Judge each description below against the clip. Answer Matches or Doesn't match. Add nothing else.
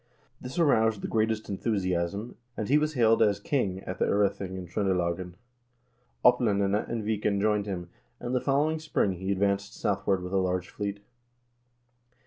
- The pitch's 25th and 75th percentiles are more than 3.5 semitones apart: Doesn't match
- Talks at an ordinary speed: Matches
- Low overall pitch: Matches